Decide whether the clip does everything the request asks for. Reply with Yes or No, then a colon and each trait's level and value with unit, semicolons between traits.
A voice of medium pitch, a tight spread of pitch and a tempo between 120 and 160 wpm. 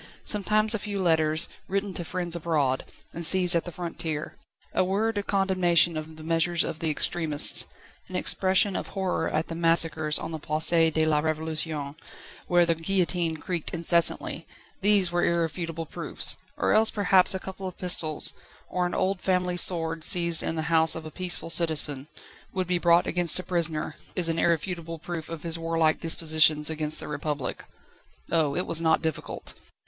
No: medium, 165 Hz; narrow, 2.3 semitones; average, 175 wpm